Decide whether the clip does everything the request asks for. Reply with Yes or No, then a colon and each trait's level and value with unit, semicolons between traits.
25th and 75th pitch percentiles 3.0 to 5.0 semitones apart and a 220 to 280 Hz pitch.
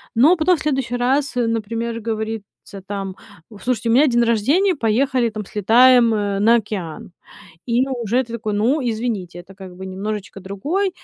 Yes: average, 3.7 semitones; high, 230 Hz